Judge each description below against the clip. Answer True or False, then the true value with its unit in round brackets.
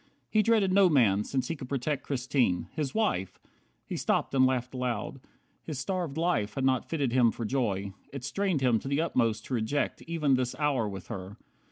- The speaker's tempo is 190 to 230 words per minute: True (195 wpm)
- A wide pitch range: False (4.4 semitones)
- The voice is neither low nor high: False (130 Hz)